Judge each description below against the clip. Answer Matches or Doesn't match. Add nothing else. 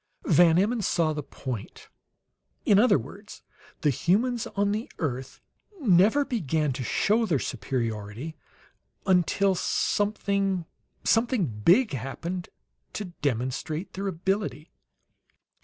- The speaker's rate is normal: Doesn't match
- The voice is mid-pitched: Matches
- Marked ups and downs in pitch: Matches